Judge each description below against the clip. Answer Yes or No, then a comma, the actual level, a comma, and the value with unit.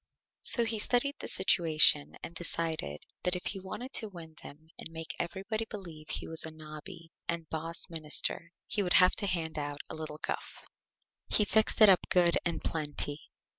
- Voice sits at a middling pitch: Yes, medium, 170 Hz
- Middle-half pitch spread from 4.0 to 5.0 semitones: No, average, 3.4 semitones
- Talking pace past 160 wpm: Yes, average, 180 wpm